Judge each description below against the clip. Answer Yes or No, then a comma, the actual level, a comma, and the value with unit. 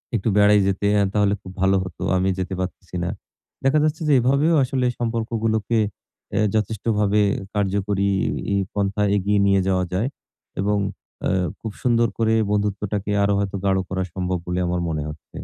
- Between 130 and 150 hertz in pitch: No, low, 100 Hz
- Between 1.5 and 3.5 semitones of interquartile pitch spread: Yes, average, 2.7 semitones